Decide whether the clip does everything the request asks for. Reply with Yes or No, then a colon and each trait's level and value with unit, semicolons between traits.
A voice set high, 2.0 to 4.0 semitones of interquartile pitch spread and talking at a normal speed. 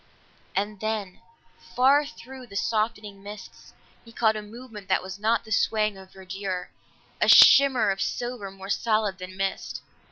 Yes: high, 210 Hz; average, 2.9 semitones; average, 155 wpm